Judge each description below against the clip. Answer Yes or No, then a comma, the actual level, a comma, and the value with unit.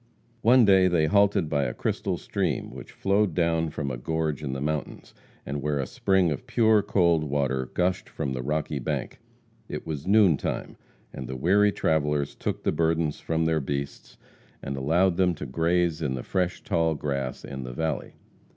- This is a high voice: No, very low, 80 Hz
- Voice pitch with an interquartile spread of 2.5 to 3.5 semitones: No, average, 4.2 semitones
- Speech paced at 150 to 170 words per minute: No, average, 185 wpm